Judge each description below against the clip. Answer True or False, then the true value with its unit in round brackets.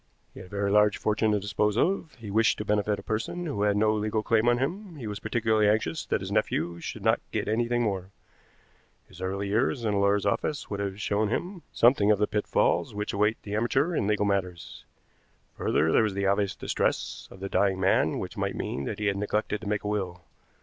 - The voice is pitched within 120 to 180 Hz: False (105 Hz)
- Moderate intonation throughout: False (1.8 semitones)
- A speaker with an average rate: False (225 wpm)